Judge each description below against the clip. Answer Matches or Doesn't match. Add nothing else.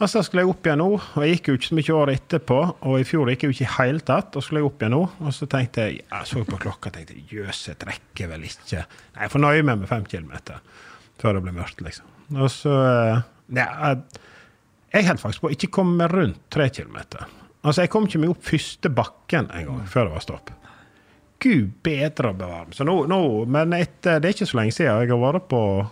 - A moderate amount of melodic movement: Doesn't match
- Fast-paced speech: Matches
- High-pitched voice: Doesn't match